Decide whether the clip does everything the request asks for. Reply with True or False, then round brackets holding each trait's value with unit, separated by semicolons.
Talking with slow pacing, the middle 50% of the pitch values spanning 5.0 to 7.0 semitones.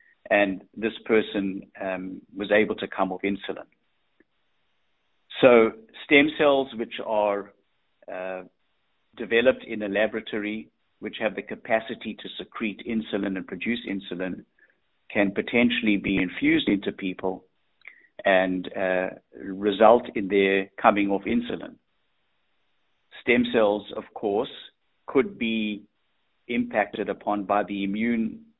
False (115 wpm; 2.8 semitones)